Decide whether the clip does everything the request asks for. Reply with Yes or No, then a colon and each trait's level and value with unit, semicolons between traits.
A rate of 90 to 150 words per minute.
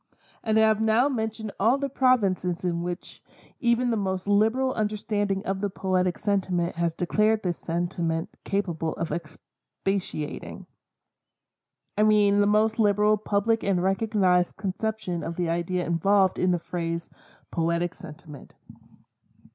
Yes: slow, 135 wpm